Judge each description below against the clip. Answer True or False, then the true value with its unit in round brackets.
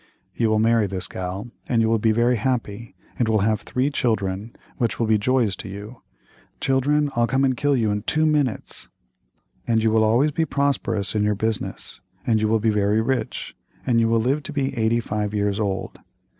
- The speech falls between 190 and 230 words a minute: True (205 wpm)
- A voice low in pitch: True (115 Hz)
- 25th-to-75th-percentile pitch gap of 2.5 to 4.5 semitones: True (3.3 semitones)